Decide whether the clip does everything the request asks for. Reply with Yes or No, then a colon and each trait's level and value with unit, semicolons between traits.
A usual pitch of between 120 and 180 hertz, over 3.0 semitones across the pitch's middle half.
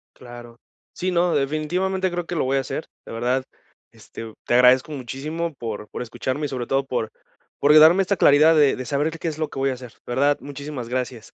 Yes: medium, 140 Hz; average, 4.0 semitones